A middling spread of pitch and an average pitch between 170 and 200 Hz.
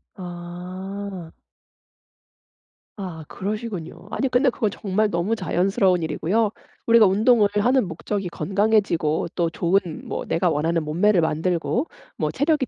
Yes: average, 3.9 semitones; high, 190 Hz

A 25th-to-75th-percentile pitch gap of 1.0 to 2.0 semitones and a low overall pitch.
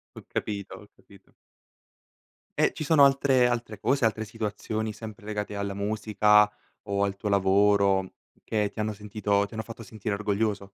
Yes: narrow, 1.6 semitones; low, 105 Hz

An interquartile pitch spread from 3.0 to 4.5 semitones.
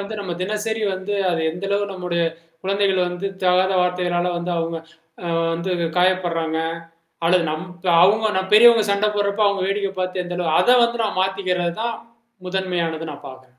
No: narrow, 2.5 semitones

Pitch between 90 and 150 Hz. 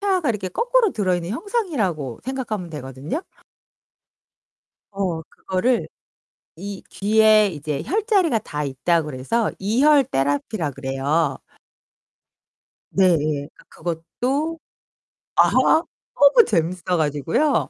No: high, 195 Hz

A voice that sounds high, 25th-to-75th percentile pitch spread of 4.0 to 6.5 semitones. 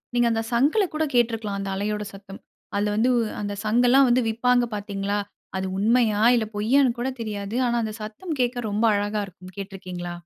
No: high, 215 Hz; average, 3.1 semitones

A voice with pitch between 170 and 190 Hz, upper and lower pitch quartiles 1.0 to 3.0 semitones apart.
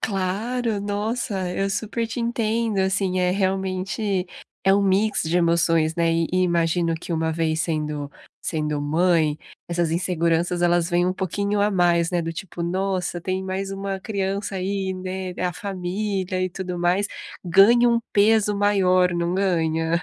Yes: medium, 185 Hz; narrow, 2.6 semitones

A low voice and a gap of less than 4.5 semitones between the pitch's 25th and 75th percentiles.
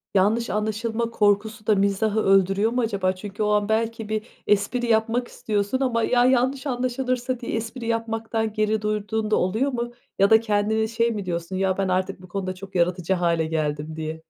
No: high, 215 Hz; average, 3.0 semitones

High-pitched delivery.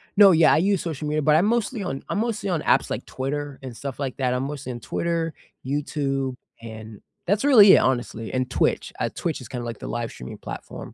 No: medium, 145 Hz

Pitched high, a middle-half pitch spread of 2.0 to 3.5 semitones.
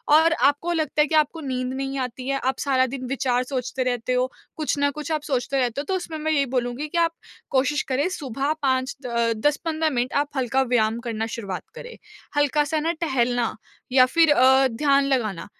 Yes: very high, 265 Hz; average, 3.1 semitones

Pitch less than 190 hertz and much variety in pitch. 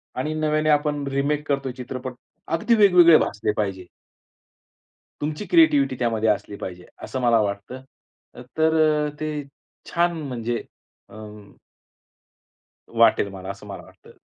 Yes: medium, 140 Hz; wide, 6.3 semitones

